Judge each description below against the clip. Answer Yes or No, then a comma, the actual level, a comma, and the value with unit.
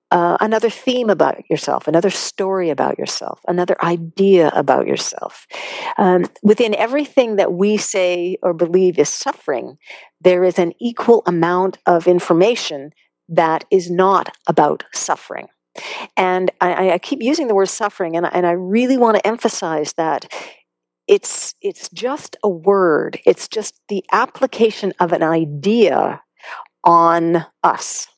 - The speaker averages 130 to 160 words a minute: Yes, average, 140 wpm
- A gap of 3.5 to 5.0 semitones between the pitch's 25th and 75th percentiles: Yes, average, 4.2 semitones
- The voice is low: No, medium, 185 Hz